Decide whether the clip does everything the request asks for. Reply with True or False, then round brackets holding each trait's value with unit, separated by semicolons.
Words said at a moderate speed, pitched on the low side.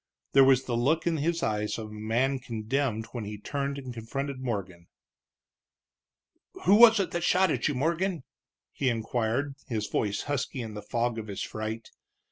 True (175 wpm; 125 Hz)